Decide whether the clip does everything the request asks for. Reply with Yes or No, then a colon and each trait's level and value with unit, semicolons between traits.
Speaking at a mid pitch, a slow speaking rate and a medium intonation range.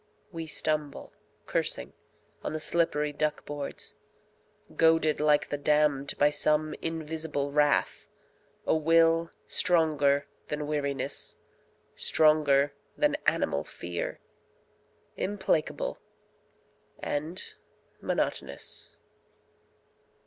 No: medium, 150 Hz; slow, 85 wpm; narrow, 1.8 semitones